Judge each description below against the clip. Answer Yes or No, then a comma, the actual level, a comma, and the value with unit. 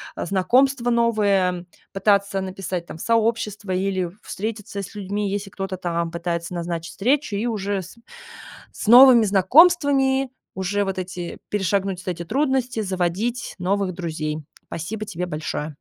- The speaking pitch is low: No, high, 195 Hz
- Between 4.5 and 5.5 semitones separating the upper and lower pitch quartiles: No, average, 3.8 semitones